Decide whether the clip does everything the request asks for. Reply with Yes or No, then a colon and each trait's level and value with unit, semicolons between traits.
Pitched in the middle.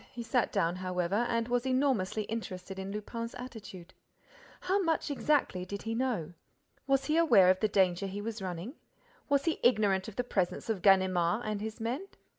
No: high, 215 Hz